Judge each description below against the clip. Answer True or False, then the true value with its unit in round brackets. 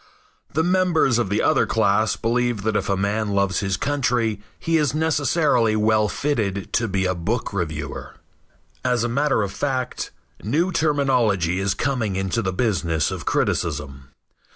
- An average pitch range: False (5.7 semitones)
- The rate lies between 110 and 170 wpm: True (155 wpm)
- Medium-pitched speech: False (110 Hz)